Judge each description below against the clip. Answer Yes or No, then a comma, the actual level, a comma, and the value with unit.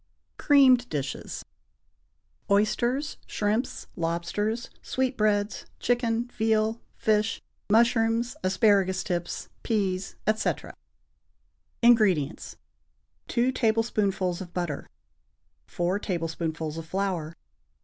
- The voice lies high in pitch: Yes, high, 210 Hz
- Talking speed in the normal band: No, slow, 75 wpm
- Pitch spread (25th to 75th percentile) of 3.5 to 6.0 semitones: Yes, average, 4.4 semitones